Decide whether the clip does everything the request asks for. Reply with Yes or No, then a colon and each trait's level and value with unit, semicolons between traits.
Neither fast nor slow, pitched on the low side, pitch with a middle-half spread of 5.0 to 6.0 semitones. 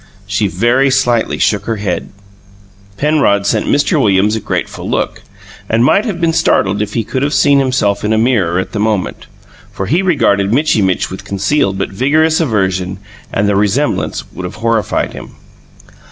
Yes: average, 175 wpm; low, 110 Hz; wide, 5.6 semitones